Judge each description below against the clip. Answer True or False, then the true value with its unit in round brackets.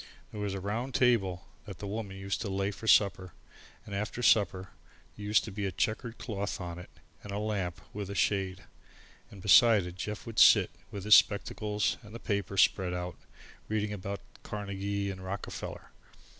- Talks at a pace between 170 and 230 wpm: True (185 wpm)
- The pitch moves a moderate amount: False (1.8 semitones)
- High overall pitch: False (100 Hz)